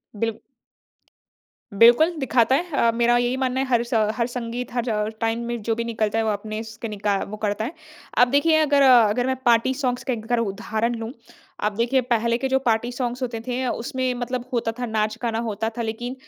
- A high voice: Yes, high, 235 Hz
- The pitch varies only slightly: Yes, narrow, 2.1 semitones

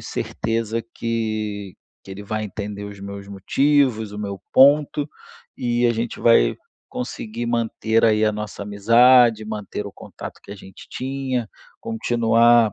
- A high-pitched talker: No, low, 110 Hz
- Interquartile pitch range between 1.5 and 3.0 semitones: Yes, narrow, 2.5 semitones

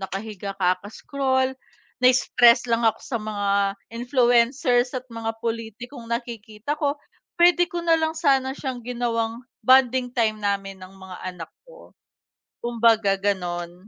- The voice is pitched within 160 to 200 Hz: No, high, 235 Hz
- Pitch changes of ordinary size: Yes, average, 4.1 semitones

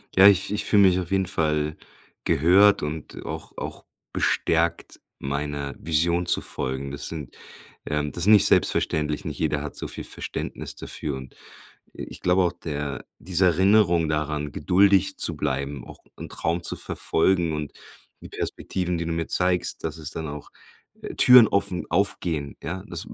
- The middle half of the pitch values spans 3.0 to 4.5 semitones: Yes, average, 3.7 semitones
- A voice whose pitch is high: No, very low, 80 Hz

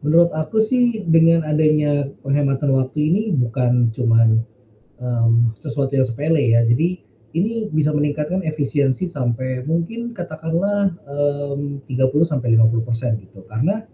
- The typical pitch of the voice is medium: Yes, medium, 145 Hz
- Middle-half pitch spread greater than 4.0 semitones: Yes, average, 4.7 semitones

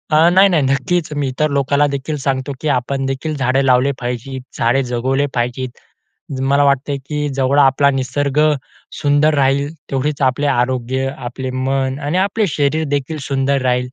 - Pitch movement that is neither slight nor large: No, narrow, 1.7 semitones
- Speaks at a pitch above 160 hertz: No, low, 135 Hz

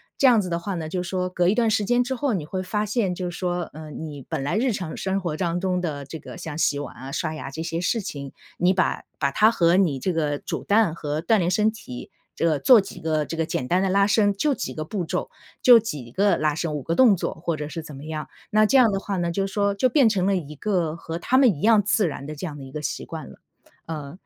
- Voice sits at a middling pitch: Yes, medium, 180 Hz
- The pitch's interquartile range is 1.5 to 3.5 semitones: No, average, 4.6 semitones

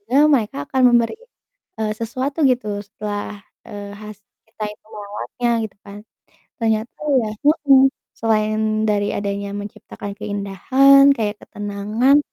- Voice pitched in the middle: No, high, 215 Hz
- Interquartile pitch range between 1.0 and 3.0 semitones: No, average, 3.4 semitones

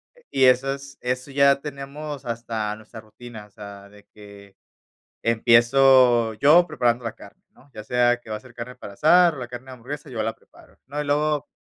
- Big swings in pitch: No, average, 3.7 semitones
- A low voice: Yes, low, 125 Hz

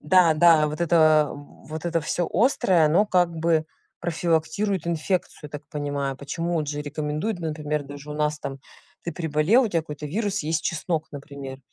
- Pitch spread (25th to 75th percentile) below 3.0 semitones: Yes, narrow, 2.5 semitones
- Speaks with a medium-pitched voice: Yes, medium, 155 Hz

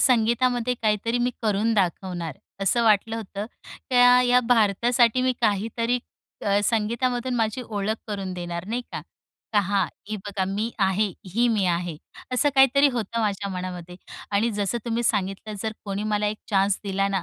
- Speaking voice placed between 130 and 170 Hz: No, high, 215 Hz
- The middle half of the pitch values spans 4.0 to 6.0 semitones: No, average, 3.3 semitones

